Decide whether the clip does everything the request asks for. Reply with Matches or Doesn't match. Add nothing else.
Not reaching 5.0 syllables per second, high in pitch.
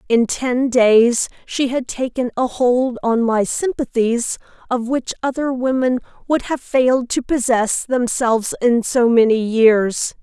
Matches